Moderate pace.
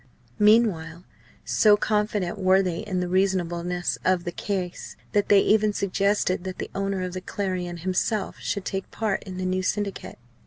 Yes: average, 165 wpm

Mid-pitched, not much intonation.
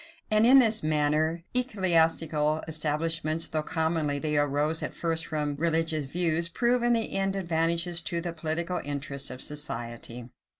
Yes: medium, 160 Hz; narrow, 2.3 semitones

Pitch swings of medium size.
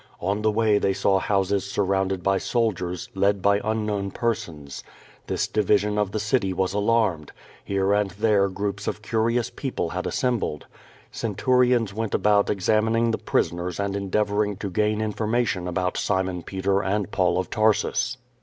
No: narrow, 2.1 semitones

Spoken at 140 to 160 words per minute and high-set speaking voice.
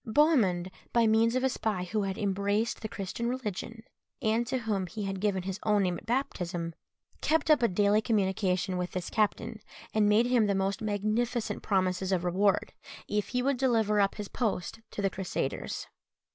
No: average, 185 wpm; high, 210 Hz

